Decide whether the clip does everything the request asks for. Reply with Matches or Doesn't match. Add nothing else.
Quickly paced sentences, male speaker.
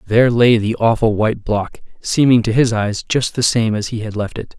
Matches